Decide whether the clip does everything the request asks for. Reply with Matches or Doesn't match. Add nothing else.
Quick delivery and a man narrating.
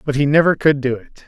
Matches